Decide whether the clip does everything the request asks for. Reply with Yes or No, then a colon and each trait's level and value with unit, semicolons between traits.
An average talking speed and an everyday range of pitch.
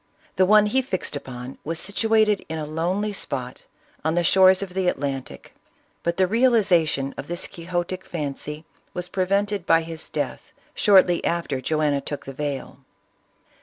Yes: average, 155 wpm; average, 4.4 semitones